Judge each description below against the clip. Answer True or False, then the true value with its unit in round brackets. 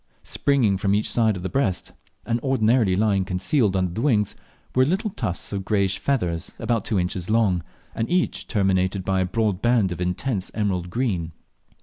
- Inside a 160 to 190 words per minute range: True (180 wpm)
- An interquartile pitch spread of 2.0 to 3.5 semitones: False (4.0 semitones)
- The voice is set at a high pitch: False (100 Hz)